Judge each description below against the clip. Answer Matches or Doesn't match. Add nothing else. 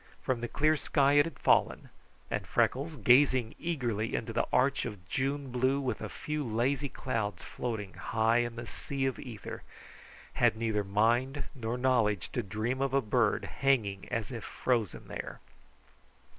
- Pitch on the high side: Doesn't match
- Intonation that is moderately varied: Matches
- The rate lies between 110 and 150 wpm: Doesn't match